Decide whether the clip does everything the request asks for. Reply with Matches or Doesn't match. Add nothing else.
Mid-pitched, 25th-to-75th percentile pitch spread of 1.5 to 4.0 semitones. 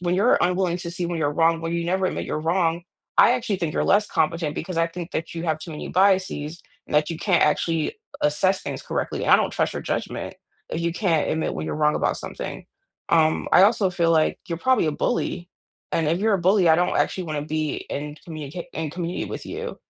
Matches